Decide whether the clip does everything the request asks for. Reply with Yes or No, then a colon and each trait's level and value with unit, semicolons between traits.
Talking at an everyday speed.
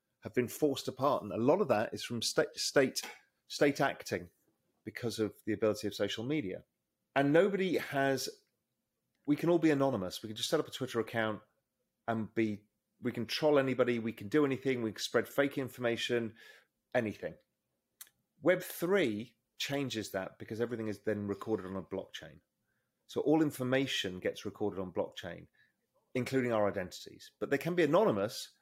Yes: average, 170 wpm